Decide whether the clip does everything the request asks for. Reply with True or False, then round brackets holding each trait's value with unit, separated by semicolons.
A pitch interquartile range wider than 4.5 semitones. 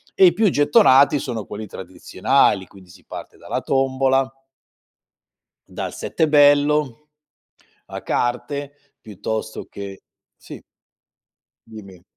True (5.2 semitones)